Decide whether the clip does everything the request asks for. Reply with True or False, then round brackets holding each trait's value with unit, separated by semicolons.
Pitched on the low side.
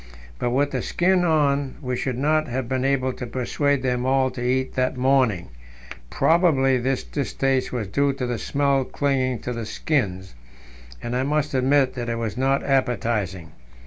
True (130 Hz)